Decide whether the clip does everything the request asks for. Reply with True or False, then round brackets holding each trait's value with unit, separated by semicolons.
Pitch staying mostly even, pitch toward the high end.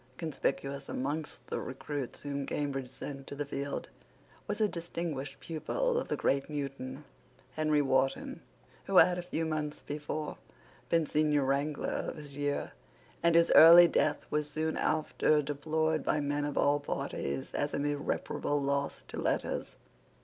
False (2.0 semitones; 145 Hz)